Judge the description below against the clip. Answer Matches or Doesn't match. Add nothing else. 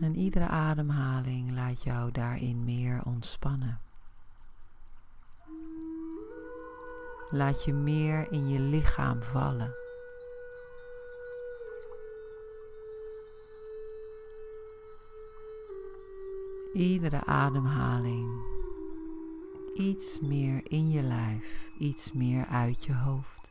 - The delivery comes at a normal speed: Doesn't match